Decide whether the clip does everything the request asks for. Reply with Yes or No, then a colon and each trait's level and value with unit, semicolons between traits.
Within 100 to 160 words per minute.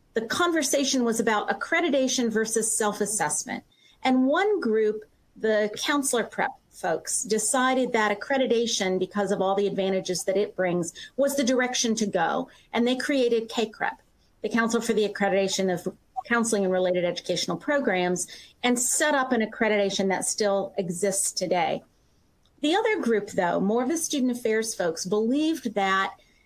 Yes: average, 150 wpm